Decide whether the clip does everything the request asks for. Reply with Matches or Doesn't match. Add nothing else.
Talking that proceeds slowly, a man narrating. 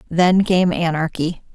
Doesn't match